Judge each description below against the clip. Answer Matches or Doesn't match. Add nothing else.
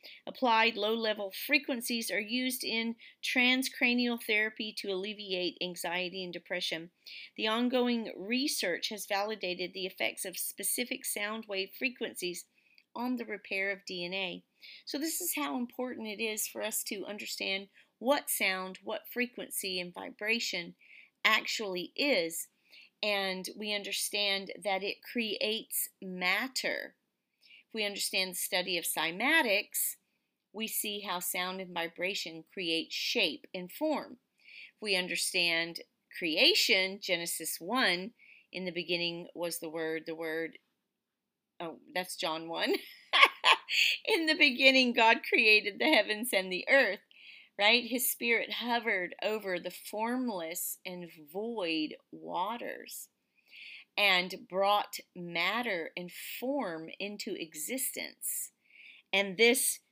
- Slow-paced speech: Matches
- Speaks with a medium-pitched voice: Doesn't match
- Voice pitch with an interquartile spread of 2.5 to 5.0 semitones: Doesn't match